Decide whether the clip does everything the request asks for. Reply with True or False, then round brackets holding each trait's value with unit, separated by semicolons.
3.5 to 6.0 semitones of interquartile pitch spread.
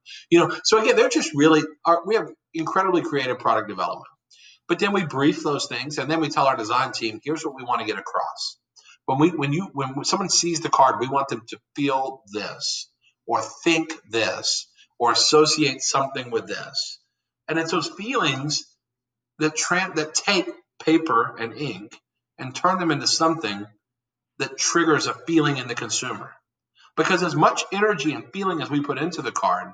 True (4.1 semitones)